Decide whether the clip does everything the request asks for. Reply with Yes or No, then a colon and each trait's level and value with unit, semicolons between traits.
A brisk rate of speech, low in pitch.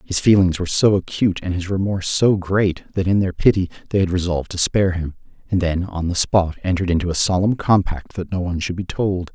Yes: fast, 230 wpm; very low, 90 Hz